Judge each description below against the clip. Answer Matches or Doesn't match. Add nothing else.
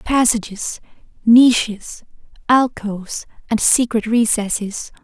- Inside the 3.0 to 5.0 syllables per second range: Matches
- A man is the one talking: Doesn't match